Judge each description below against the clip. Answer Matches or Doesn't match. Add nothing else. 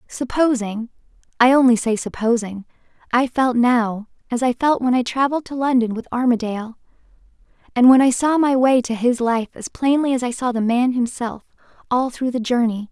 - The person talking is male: Doesn't match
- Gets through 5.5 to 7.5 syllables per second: Doesn't match